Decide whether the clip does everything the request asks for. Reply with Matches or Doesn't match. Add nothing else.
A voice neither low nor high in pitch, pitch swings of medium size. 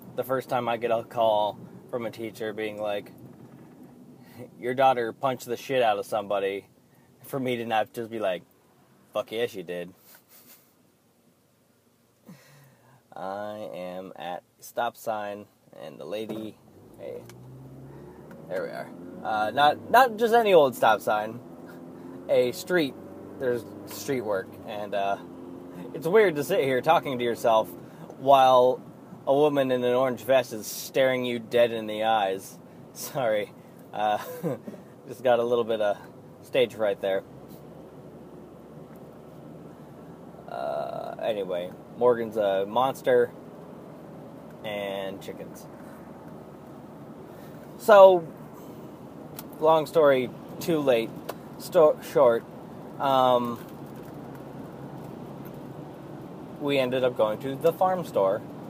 Doesn't match